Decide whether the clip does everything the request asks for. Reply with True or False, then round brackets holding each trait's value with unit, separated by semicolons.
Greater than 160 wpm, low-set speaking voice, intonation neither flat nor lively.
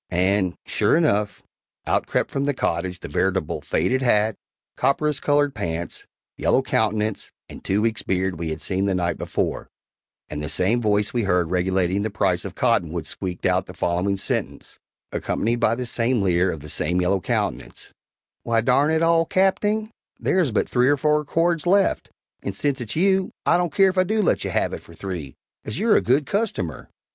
False (195 wpm; 110 Hz; 8.0 semitones)